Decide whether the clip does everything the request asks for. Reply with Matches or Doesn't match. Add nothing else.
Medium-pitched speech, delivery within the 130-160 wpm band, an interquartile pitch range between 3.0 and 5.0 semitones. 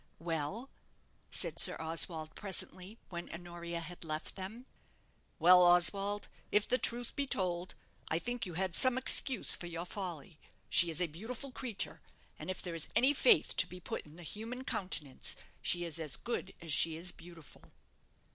Doesn't match